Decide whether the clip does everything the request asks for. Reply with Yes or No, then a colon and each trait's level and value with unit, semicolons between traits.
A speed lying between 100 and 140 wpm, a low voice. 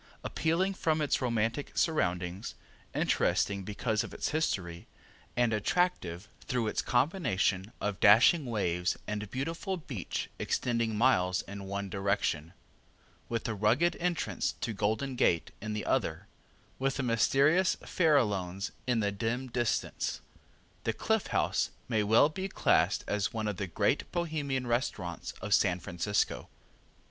Yes: slow, 135 wpm; low, 110 Hz